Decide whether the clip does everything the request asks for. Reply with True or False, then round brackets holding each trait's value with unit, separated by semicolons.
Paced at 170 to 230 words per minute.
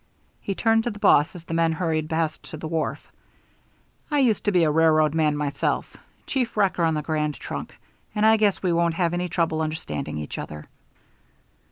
True (195 wpm)